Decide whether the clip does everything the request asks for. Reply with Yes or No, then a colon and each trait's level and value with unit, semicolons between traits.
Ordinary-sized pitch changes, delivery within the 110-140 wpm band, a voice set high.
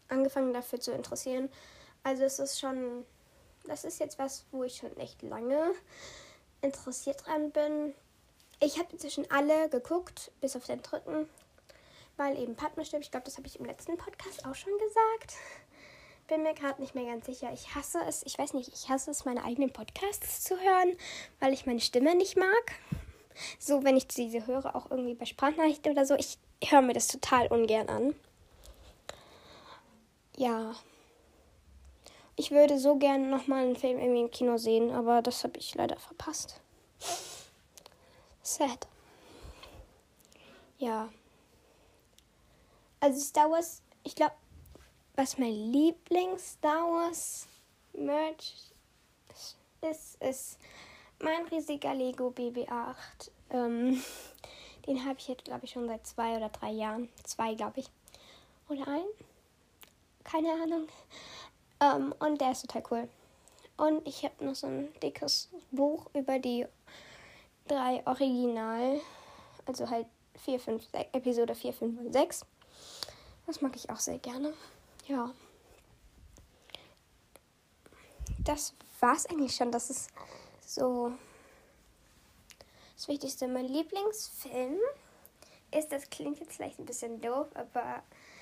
Yes: average, 3.6 semitones; average, 135 wpm; very high, 275 Hz